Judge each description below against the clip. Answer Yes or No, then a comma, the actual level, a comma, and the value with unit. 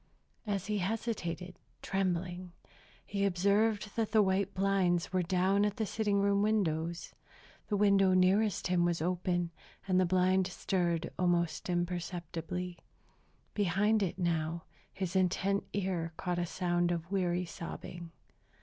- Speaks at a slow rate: Yes, slow, 130 wpm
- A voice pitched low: No, medium, 185 Hz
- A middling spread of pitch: No, narrow, 2.2 semitones